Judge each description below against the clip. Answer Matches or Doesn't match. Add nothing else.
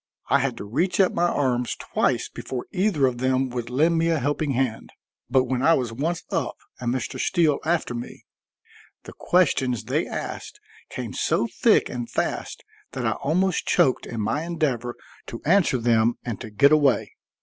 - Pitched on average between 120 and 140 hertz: Matches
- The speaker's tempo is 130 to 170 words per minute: Doesn't match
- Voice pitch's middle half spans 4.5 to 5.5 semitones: Matches